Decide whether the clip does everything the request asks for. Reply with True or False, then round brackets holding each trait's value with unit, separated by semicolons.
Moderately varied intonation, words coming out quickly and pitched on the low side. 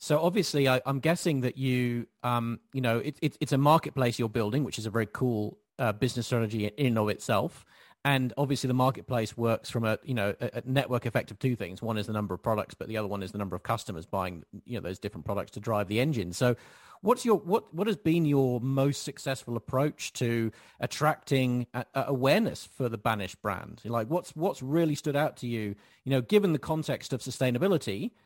True (4.0 semitones; 225 wpm; 125 Hz)